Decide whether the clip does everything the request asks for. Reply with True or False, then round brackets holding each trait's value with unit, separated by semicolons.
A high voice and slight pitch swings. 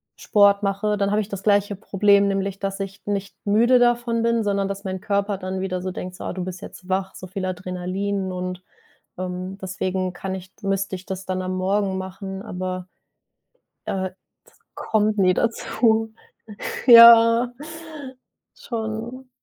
True (195 Hz; 2.1 semitones)